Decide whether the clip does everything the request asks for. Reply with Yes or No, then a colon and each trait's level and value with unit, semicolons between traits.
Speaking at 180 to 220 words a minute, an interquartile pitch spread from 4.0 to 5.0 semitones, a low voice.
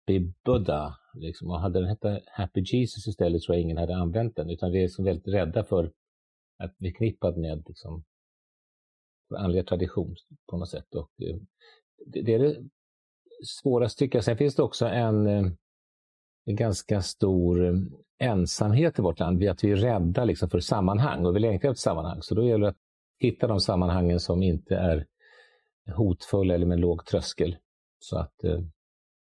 No: average, 170 wpm; average, 4.4 semitones; very low, 95 Hz